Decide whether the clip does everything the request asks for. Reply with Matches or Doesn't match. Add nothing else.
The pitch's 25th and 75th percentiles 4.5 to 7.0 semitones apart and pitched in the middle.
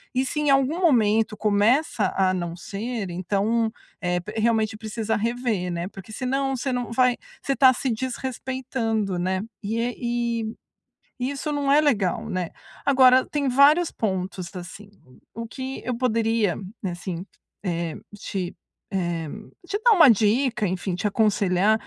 Doesn't match